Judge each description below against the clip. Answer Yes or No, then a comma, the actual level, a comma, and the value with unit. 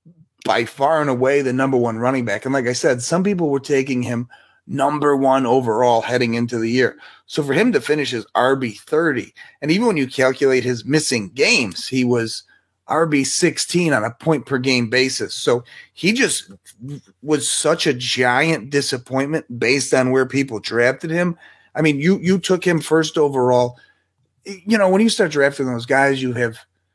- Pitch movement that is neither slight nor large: Yes, average, 3.9 semitones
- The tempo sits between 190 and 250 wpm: No, average, 180 wpm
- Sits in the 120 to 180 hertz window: Yes, low, 135 Hz